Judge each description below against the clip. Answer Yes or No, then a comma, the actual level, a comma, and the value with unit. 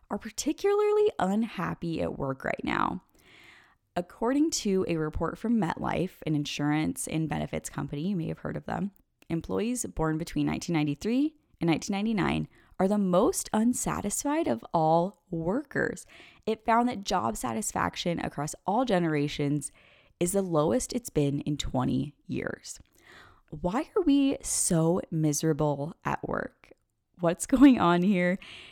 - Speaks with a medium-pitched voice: Yes, medium, 175 Hz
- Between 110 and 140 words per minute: Yes, slow, 135 wpm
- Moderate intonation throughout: No, wide, 6.5 semitones